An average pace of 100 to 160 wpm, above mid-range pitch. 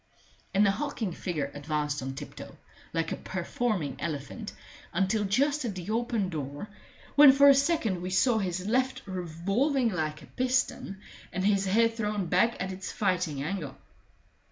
Yes: average, 155 wpm; high, 195 Hz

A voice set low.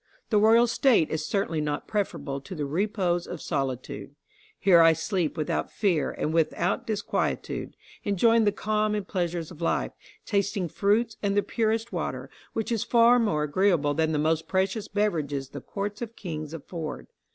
No: medium, 185 Hz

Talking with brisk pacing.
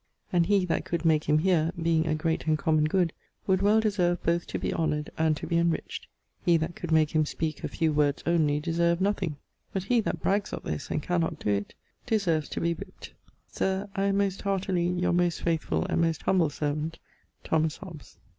Yes: fast, 210 wpm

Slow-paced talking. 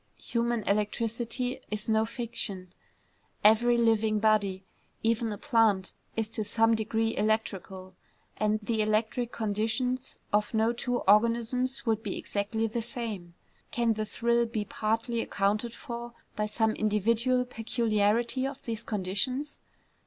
Yes: slow, 130 wpm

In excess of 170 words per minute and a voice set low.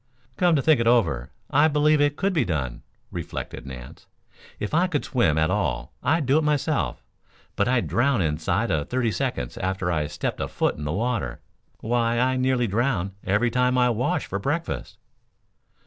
Yes: average, 180 wpm; low, 120 Hz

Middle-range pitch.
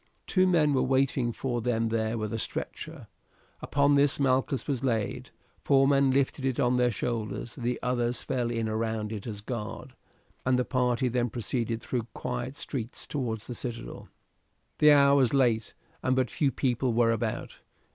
No: low, 125 Hz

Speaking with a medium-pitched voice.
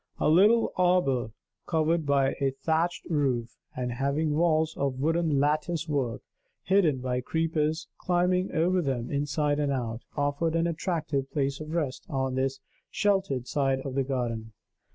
Yes: medium, 145 Hz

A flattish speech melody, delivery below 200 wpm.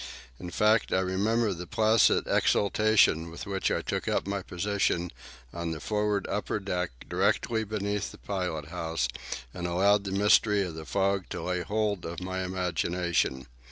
No: average, 3.0 semitones; average, 160 wpm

